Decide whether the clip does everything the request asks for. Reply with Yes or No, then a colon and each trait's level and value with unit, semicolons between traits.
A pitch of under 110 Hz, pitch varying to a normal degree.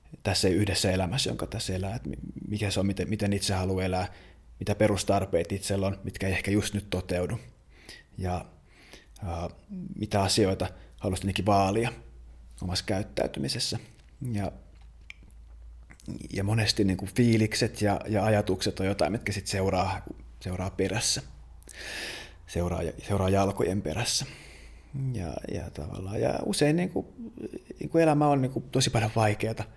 Yes: low, 100 Hz; average, 3.0 semitones